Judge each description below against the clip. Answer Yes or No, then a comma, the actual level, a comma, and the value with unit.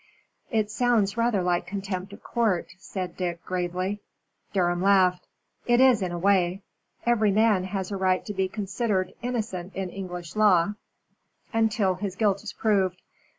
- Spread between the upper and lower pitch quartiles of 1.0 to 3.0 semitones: Yes, average, 2.7 semitones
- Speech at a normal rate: Yes, average, 150 wpm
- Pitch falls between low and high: No, high, 195 Hz